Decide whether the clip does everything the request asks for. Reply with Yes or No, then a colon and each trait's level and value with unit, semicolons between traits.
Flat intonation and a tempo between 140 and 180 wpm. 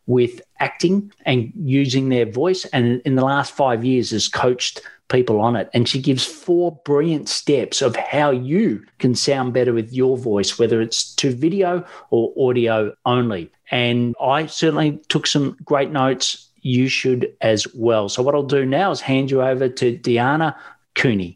No: average, 3.3 semitones; average, 175 wpm